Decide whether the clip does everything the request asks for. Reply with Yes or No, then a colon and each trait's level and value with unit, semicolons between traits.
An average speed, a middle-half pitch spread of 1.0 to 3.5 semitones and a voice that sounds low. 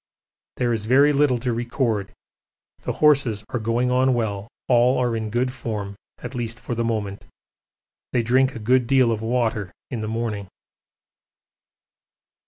Yes: average, 155 wpm; narrow, 2.4 semitones; low, 120 Hz